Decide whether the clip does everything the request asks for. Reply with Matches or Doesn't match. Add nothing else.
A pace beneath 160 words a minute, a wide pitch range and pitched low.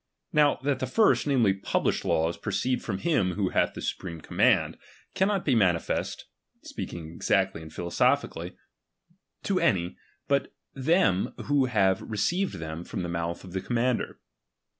Matches